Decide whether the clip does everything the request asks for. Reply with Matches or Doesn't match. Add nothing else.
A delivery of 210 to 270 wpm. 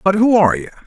Doesn't match